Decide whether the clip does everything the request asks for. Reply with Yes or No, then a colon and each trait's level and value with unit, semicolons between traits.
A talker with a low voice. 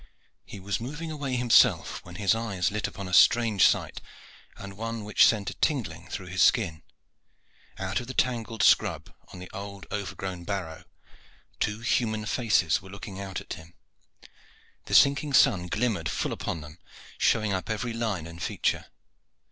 Yes: low, 100 Hz